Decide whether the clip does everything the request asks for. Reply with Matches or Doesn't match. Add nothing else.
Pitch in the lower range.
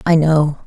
Doesn't match